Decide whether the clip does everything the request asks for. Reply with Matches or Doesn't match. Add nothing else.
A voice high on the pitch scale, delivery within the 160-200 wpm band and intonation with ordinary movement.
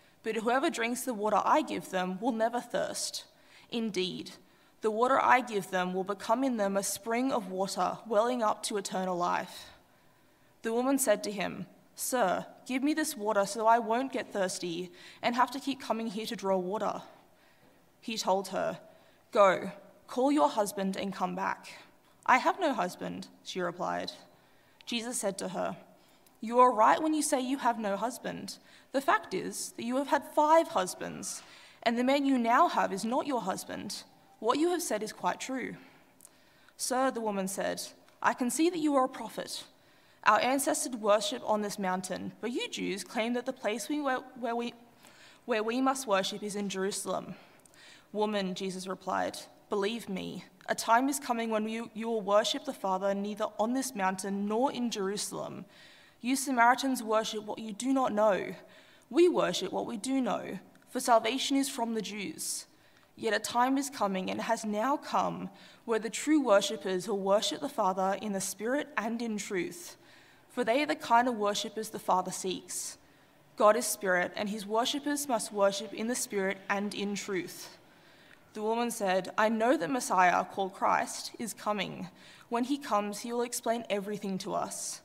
Matches